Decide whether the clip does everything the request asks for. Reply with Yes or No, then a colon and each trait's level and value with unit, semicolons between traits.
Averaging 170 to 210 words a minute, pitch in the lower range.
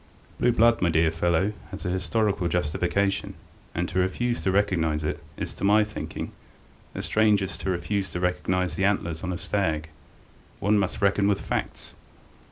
Yes: average, 175 wpm; very low, 95 Hz